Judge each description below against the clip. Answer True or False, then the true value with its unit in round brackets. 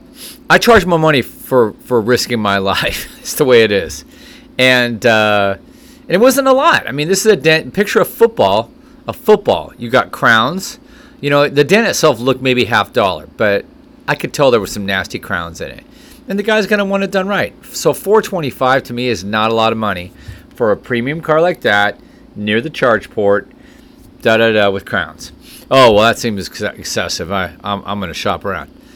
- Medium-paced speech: False (210 wpm)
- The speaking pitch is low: True (130 Hz)